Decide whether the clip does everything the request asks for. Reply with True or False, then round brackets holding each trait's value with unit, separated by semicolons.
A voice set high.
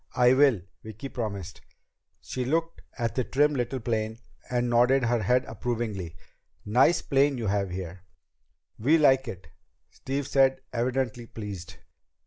False (120 Hz)